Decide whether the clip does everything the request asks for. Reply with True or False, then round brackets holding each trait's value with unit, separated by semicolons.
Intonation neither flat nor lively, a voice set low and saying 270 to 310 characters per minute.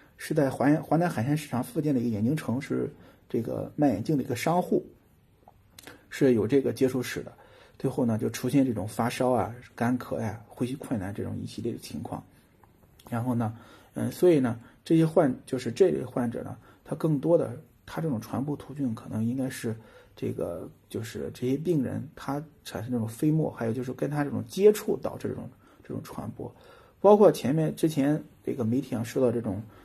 True (4.1 semitones; 125 Hz; 290 characters per minute)